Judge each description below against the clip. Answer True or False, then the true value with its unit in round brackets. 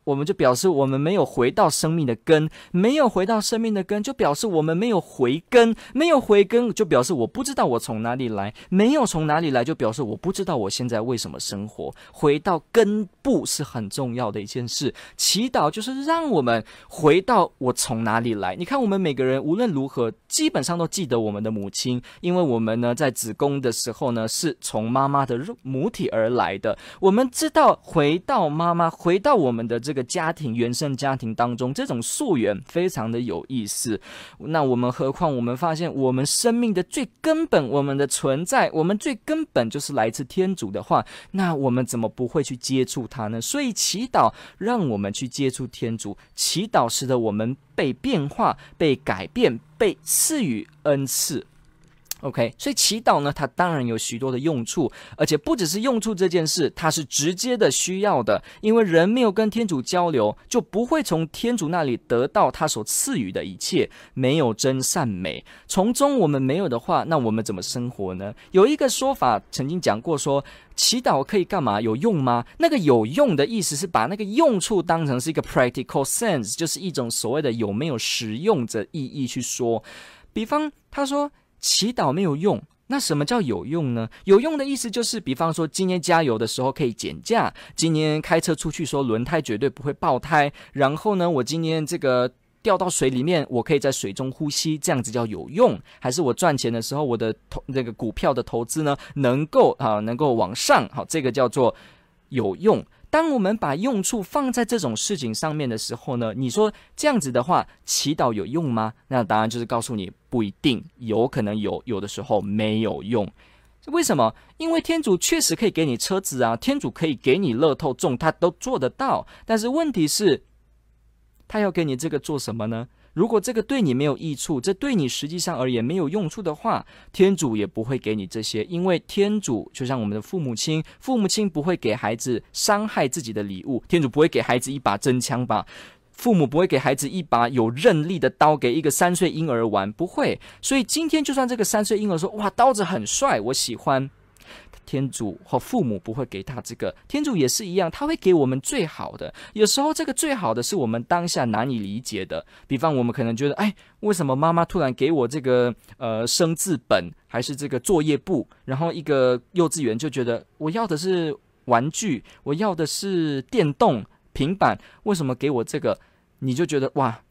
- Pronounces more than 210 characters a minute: True (300 characters per minute)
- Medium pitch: True (150 Hz)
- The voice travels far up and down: True (8.0 semitones)